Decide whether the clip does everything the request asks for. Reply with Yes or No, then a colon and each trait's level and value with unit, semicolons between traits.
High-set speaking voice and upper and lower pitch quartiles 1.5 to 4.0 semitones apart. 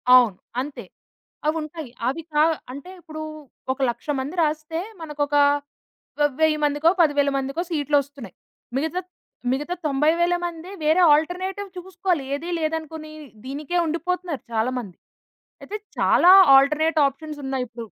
Yes: very high, 305 Hz; average, 2.9 semitones